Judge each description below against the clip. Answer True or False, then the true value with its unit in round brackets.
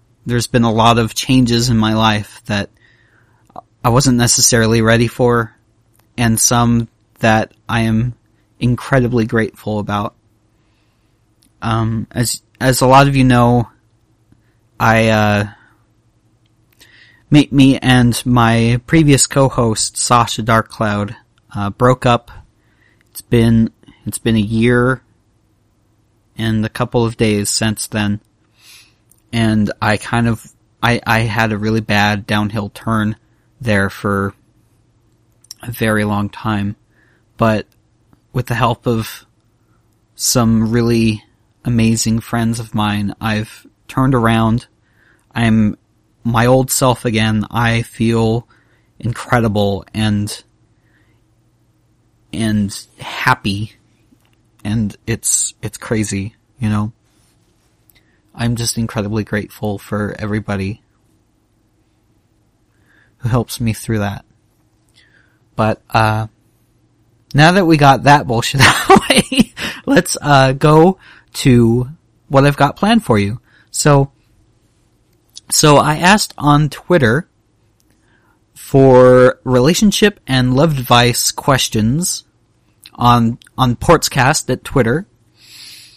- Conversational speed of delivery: False (110 wpm)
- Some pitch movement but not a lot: False (1.8 semitones)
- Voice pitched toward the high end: False (115 Hz)